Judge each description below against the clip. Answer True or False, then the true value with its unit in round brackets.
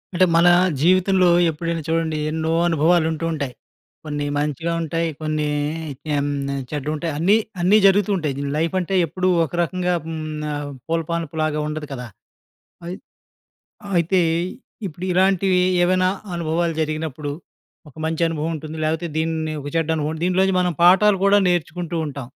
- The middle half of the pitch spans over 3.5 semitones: False (2.6 semitones)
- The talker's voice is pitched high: False (165 Hz)